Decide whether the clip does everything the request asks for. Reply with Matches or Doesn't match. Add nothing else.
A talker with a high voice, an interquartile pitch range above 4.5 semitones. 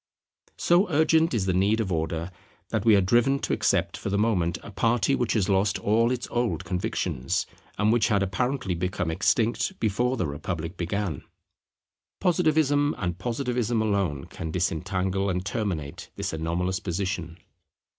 Doesn't match